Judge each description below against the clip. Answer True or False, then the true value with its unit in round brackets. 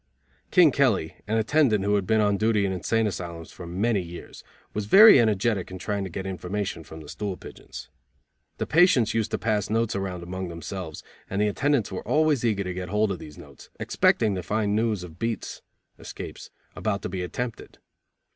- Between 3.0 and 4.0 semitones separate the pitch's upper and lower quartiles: True (3.4 semitones)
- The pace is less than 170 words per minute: False (195 wpm)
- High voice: False (100 Hz)